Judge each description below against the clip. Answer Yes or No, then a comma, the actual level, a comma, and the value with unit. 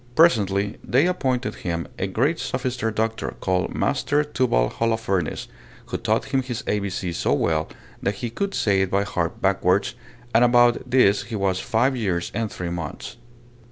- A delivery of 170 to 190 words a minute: No, average, 160 wpm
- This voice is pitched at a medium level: No, low, 105 Hz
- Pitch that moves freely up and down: No, average, 4.6 semitones